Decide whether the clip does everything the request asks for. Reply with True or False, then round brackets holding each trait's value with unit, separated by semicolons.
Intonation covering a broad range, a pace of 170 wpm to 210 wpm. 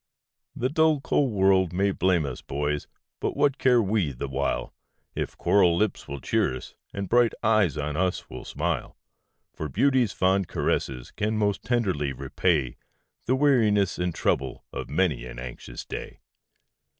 False (7.2 semitones; 150 wpm)